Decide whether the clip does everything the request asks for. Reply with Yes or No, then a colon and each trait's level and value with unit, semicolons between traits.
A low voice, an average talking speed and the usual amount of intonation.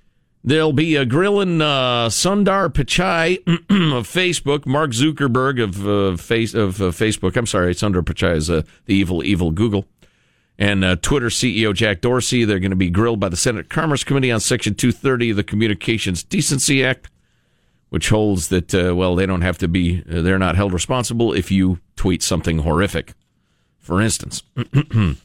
No: low, 110 Hz; average, 175 wpm; wide, 6.0 semitones